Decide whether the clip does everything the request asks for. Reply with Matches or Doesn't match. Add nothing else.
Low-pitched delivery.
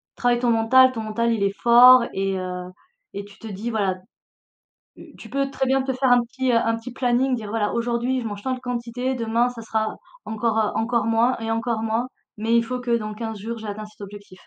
Doesn't match